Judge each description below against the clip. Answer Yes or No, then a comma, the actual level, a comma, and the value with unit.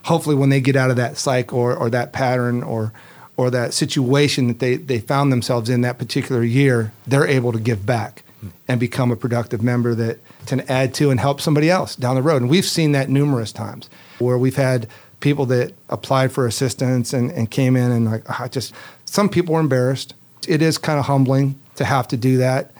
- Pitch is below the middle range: Yes, low, 130 Hz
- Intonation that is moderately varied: No, narrow, 2.2 semitones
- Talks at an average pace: No, fast, 220 wpm